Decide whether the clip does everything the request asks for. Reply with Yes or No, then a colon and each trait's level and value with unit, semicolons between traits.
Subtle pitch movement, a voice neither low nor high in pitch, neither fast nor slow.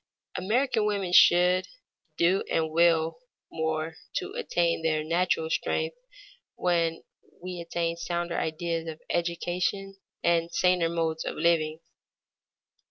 No: narrow, 1.9 semitones; medium, 170 Hz; slow, 115 wpm